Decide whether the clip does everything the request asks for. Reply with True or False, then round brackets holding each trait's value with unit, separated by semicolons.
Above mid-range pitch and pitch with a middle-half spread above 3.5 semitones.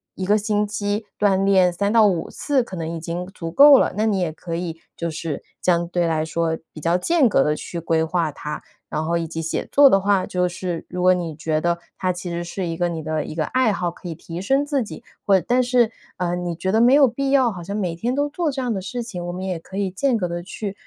False (180 Hz; 4.2 semitones)